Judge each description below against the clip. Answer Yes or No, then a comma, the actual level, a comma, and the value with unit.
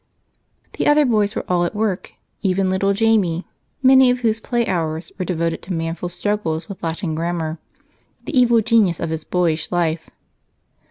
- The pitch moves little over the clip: No, average, 4.9 semitones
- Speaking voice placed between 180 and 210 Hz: Yes, medium, 185 Hz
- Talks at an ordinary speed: Yes, average, 165 wpm